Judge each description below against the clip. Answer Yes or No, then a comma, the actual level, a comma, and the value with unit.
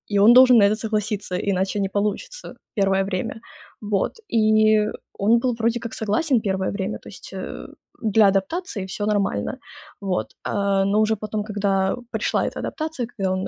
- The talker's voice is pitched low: No, high, 210 Hz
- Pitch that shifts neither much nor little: No, narrow, 2.2 semitones